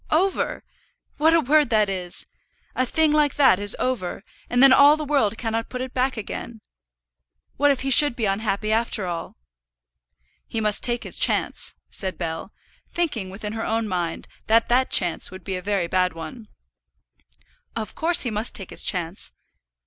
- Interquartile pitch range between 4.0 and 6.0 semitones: Yes, average, 5.2 semitones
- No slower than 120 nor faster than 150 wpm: No, average, 175 wpm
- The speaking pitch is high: Yes, high, 225 Hz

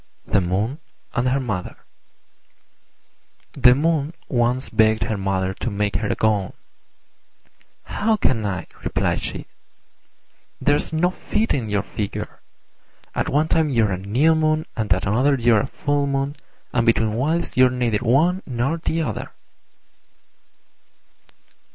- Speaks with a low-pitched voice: Yes, low, 125 Hz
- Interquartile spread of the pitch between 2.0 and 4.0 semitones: No, wide, 5.5 semitones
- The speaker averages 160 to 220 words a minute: No, slow, 135 wpm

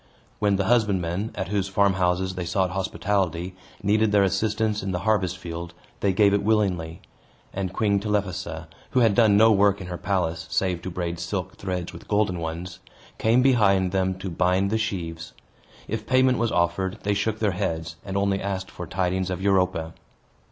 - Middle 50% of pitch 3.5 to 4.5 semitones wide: No, narrow, 2.4 semitones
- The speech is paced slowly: No, average, 180 wpm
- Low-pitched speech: Yes, very low, 95 Hz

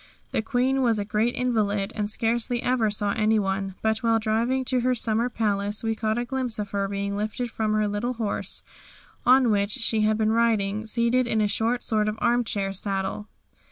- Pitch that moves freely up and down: No, narrow, 2.5 semitones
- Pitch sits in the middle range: No, high, 220 Hz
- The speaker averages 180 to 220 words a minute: Yes, average, 190 wpm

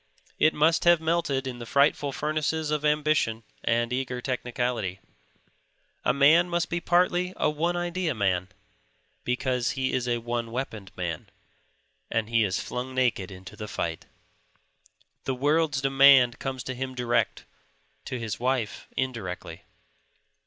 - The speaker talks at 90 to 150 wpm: Yes, average, 140 wpm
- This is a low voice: Yes, low, 130 Hz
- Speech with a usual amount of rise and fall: Yes, average, 4.4 semitones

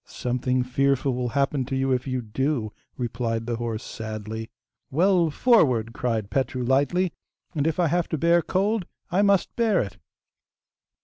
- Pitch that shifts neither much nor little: No, wide, 6.0 semitones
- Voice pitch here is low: Yes, low, 130 Hz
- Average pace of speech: Yes, average, 160 wpm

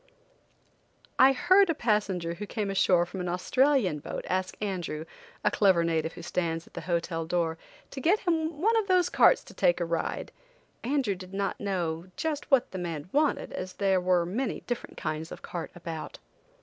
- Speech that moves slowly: No, average, 190 wpm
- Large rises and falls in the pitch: Yes, wide, 7.9 semitones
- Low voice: No, high, 190 Hz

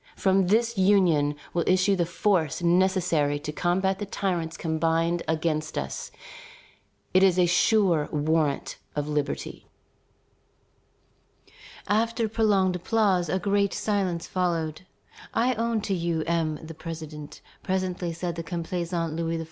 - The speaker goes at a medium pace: No, slow, 130 wpm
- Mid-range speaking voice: Yes, medium, 175 Hz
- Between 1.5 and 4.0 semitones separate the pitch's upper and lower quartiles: Yes, average, 2.9 semitones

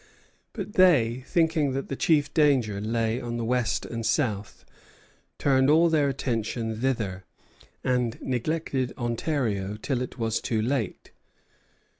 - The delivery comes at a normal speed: No, slow, 130 wpm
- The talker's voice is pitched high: No, low, 125 Hz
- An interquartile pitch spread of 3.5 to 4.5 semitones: Yes, average, 4.1 semitones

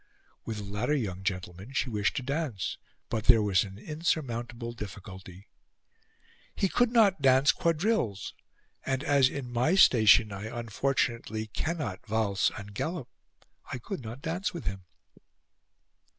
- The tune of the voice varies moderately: No, wide, 5.8 semitones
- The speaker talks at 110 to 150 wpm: Yes, slow, 135 wpm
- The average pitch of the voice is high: No, low, 120 Hz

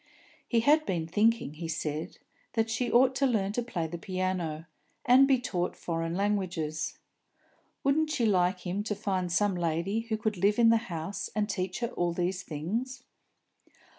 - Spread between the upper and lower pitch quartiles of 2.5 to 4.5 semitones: No, average, 4.9 semitones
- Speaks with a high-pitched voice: Yes, high, 195 Hz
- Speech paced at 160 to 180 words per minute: Yes, average, 170 wpm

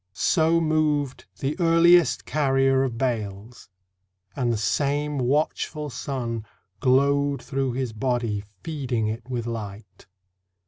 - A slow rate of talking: Yes, slow, 110 wpm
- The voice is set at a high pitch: No, low, 135 Hz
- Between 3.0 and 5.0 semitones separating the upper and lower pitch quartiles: Yes, average, 4.0 semitones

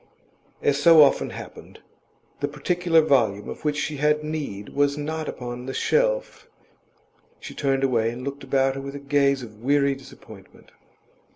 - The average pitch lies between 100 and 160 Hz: Yes, medium, 140 Hz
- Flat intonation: Yes, narrow, 2.1 semitones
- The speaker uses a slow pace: No, average, 160 wpm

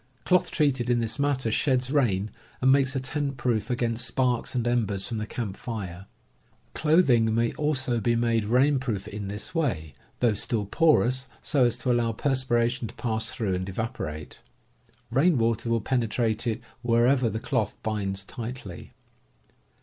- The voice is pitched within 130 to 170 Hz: No, low, 120 Hz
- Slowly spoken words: No, average, 160 wpm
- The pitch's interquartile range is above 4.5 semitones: No, average, 3.1 semitones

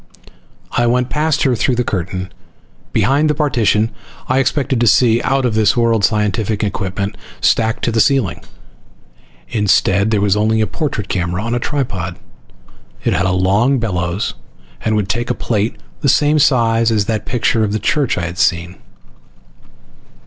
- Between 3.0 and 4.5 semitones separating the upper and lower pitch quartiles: Yes, average, 3.7 semitones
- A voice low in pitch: Yes, low, 110 Hz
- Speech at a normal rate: Yes, average, 165 wpm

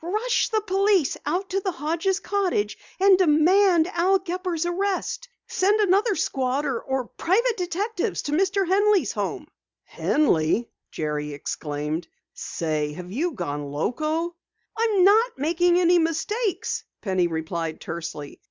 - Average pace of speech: No, slow, 130 wpm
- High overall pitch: Yes, very high, 345 Hz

